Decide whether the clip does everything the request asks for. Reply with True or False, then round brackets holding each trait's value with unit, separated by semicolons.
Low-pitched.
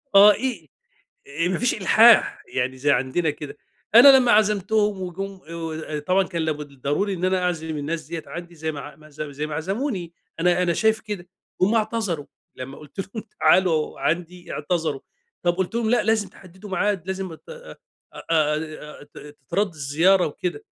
False (175 Hz)